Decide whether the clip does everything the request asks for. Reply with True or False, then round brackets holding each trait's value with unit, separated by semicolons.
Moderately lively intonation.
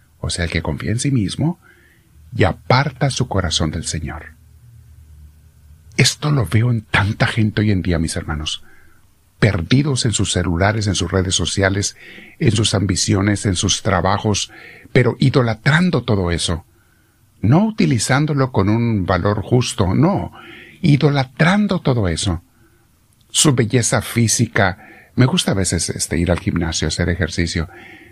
False (6.3 semitones)